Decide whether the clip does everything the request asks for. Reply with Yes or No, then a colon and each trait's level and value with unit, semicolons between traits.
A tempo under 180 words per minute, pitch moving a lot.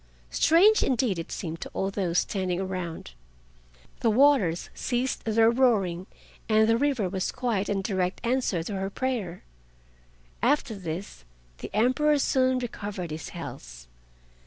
Yes: slow, 135 wpm; wide, 5.7 semitones